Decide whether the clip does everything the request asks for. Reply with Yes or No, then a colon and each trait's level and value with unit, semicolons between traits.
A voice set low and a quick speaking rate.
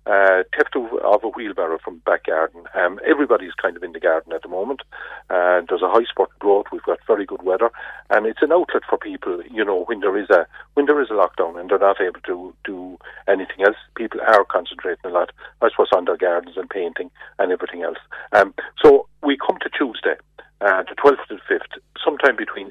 No: medium, 170 Hz; fast, 220 wpm